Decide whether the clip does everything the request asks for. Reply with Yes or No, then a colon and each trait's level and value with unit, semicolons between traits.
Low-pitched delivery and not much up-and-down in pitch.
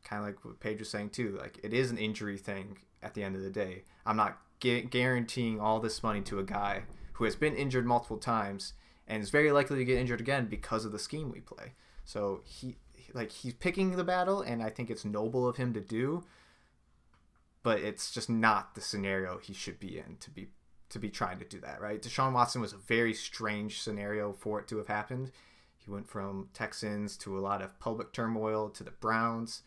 No: low, 110 Hz; average, 3.1 semitones